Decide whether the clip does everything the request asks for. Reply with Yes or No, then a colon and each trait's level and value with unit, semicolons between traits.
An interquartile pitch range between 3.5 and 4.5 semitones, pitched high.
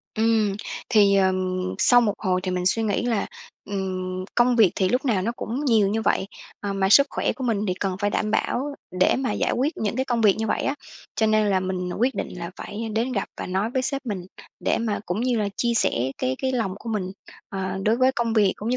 Yes: average, 3.8 semitones; high, 215 Hz